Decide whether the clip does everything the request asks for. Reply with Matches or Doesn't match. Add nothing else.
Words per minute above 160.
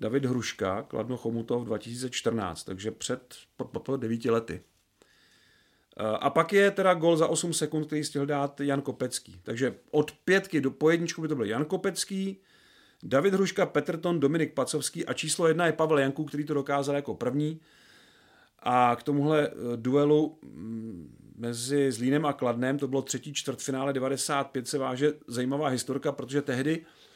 Doesn't match